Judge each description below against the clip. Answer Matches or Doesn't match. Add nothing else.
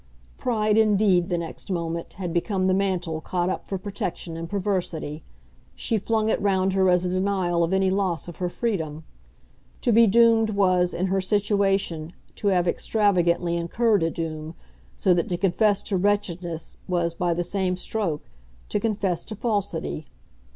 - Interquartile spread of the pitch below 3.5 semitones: Matches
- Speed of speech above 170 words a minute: Doesn't match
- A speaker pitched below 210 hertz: Matches